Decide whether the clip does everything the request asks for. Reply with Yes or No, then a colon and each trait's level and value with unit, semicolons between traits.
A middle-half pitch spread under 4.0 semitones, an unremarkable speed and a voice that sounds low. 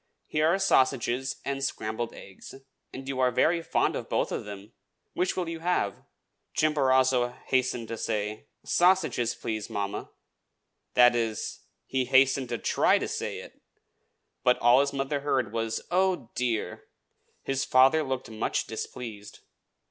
Yes: average, 3.3 semitones; average, 145 wpm; low, 130 Hz